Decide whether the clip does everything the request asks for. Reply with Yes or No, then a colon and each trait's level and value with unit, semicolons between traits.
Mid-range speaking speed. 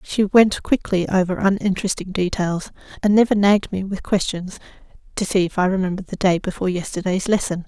Yes: average, 170 wpm